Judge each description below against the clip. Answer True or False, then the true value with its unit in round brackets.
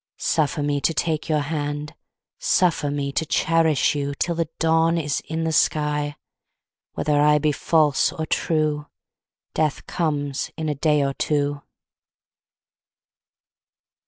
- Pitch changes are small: True (1.8 semitones)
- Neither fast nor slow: False (130 wpm)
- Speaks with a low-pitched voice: False (150 Hz)